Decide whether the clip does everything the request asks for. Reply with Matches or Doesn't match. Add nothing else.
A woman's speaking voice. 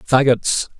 Doesn't match